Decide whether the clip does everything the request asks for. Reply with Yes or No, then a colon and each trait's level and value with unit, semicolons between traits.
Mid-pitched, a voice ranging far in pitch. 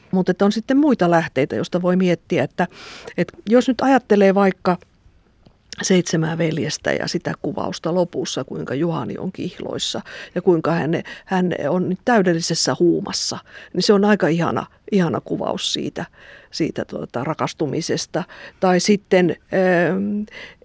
No: medium, 180 Hz; average, 3.2 semitones